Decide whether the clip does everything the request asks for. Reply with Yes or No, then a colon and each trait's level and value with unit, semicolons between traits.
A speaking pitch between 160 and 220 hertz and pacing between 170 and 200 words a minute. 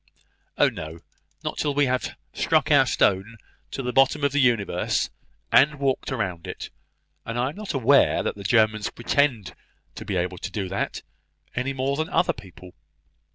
No: low, 120 Hz; average, 175 wpm